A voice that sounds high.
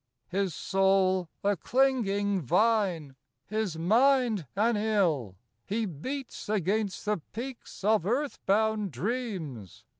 Yes: high, 205 Hz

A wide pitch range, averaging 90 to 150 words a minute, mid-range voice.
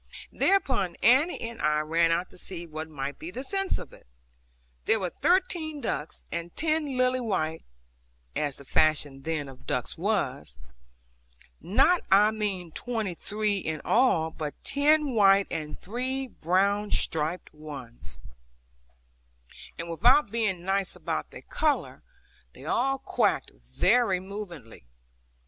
No: wide, 7.7 semitones; slow, 135 wpm; high, 195 Hz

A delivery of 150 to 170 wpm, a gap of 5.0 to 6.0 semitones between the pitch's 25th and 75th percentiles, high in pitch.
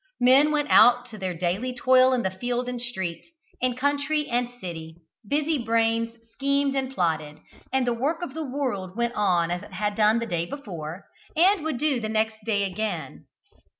No: average, 185 wpm; wide, 5.4 semitones; high, 240 Hz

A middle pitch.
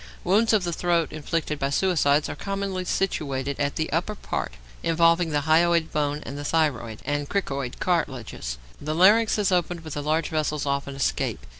Yes: medium, 155 Hz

